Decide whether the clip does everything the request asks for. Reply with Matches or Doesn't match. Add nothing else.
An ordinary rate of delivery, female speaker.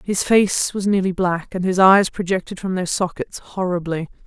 Matches